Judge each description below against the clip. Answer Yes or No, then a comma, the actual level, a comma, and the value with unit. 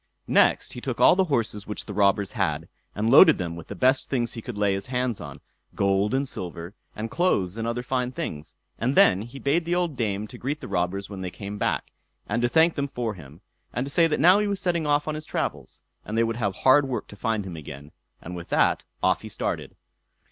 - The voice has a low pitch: Yes, low, 115 Hz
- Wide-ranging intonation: Yes, wide, 6.0 semitones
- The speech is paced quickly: Yes, fast, 240 wpm